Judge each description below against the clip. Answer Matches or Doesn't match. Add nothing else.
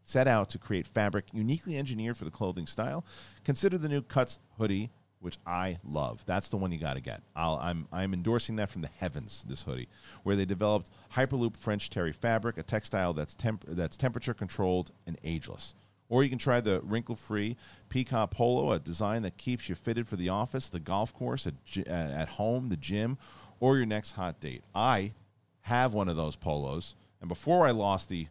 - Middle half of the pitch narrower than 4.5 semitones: Doesn't match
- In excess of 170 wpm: Matches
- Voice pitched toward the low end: Matches